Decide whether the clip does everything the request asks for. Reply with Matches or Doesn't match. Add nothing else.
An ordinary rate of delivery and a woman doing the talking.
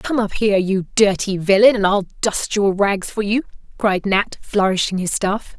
Matches